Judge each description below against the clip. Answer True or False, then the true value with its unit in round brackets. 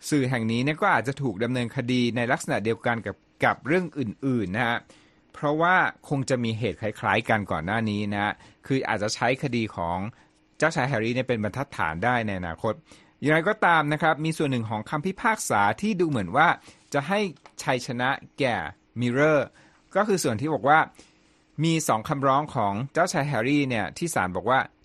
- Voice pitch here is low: True (125 Hz)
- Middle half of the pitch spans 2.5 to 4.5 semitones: False (5.2 semitones)